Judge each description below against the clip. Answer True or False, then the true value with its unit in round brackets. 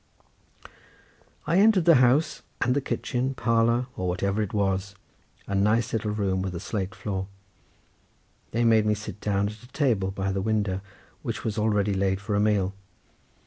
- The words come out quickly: False (170 wpm)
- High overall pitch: False (105 Hz)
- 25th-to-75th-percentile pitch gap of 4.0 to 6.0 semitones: False (3.1 semitones)